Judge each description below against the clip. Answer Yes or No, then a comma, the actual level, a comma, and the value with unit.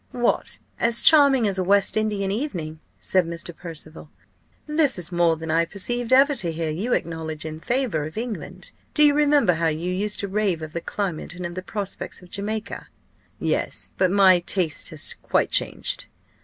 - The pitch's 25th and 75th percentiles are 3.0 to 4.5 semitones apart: No, average, 4.9 semitones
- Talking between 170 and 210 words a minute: Yes, average, 185 wpm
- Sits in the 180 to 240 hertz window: Yes, medium, 185 Hz